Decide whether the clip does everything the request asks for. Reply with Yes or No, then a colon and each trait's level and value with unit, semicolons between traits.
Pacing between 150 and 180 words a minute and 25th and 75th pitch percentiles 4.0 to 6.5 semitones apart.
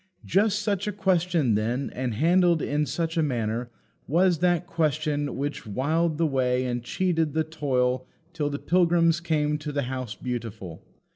Yes: average, 160 wpm; average, 5.0 semitones